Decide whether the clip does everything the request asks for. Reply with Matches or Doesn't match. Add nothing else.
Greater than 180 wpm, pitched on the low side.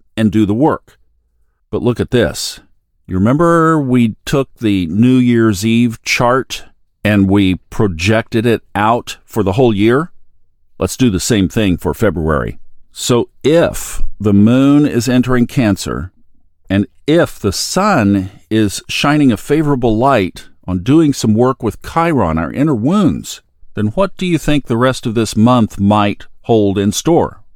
Doesn't match